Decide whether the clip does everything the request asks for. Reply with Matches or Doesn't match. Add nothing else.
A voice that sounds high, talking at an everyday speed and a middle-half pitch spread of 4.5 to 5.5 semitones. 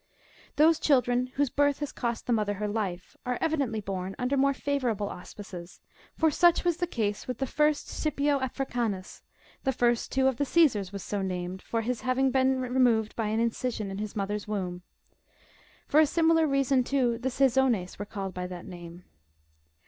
Matches